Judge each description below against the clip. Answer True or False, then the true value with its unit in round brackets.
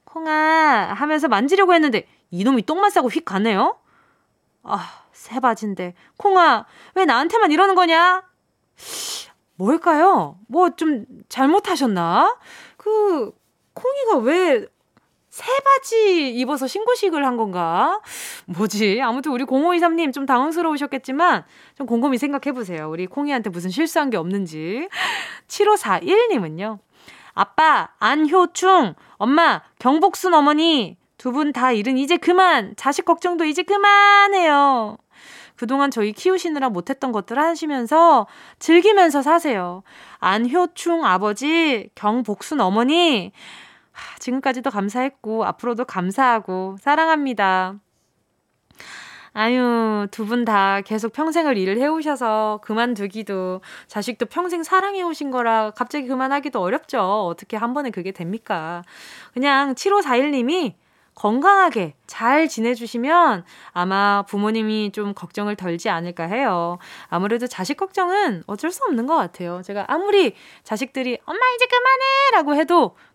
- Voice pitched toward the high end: True (270 Hz)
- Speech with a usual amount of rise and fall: False (7.9 semitones)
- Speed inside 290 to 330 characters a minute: False (275 characters per minute)